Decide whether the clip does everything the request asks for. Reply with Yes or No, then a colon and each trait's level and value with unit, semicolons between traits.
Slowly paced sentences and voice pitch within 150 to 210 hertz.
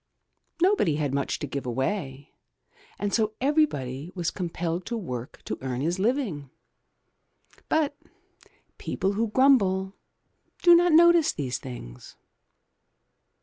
Yes: slow, 115 wpm; medium, 185 Hz